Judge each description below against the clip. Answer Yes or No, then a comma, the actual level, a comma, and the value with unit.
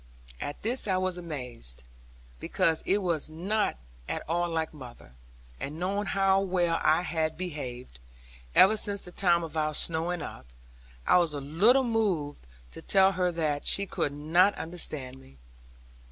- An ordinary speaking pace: Yes, average, 155 wpm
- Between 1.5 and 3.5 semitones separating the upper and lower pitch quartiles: No, average, 4.2 semitones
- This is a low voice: No, medium, 170 Hz